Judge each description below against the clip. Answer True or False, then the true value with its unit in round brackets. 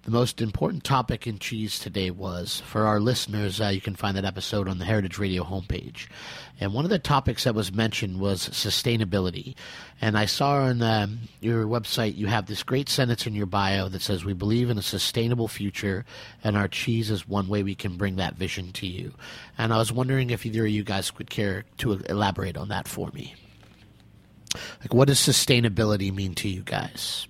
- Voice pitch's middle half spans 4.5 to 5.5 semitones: False (3.0 semitones)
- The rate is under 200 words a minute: False (205 wpm)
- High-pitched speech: False (105 Hz)